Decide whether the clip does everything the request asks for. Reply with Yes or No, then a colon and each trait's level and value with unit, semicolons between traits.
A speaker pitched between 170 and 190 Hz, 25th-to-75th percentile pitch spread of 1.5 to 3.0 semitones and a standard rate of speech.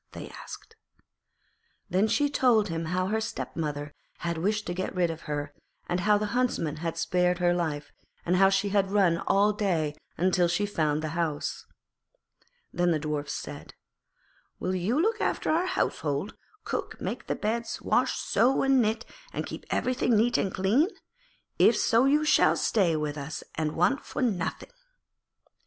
No: medium, 185 Hz; average, 5.2 semitones; average, 165 wpm